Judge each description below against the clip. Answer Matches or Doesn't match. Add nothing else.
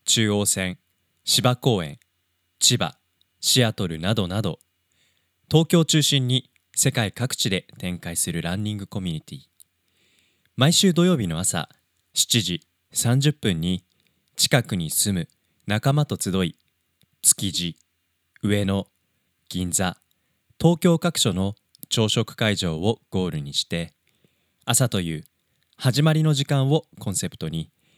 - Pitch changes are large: Matches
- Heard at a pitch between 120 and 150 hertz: Doesn't match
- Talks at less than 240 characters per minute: Matches